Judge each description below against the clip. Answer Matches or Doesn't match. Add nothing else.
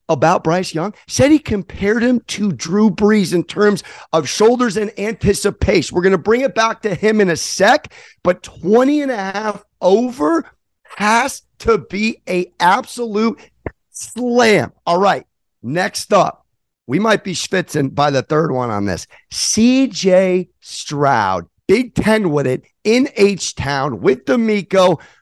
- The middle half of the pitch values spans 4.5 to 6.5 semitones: Doesn't match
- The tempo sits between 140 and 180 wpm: Matches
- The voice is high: Matches